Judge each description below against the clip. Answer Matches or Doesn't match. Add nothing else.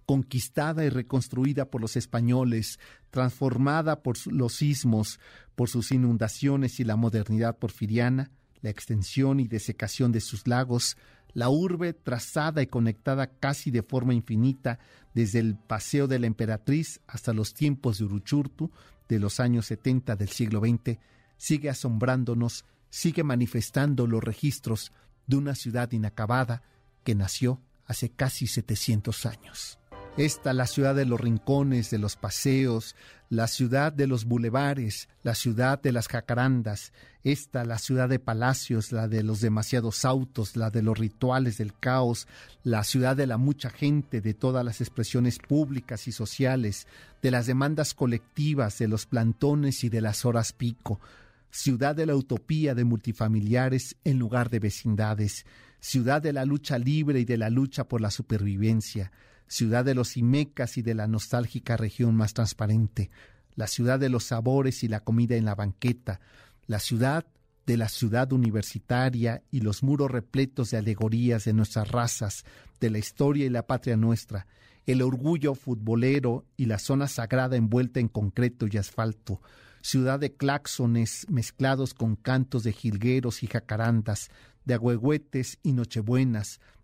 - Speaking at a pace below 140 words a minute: Doesn't match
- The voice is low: Matches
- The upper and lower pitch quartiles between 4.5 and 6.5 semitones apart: Doesn't match